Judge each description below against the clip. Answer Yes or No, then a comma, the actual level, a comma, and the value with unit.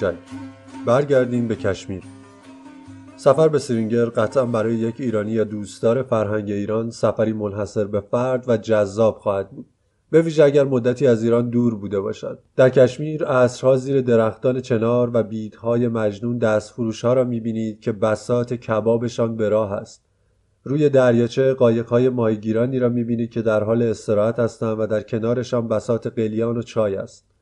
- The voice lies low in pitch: Yes, low, 115 Hz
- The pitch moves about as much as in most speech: No, narrow, 2.1 semitones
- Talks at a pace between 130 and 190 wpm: Yes, average, 150 wpm